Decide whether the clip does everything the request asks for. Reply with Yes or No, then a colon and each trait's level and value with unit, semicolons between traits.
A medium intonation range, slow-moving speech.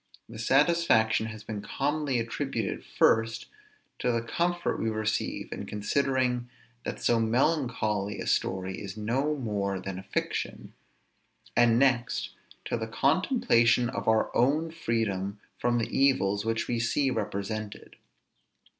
Yes: average, 3.8 semitones; slow, 130 wpm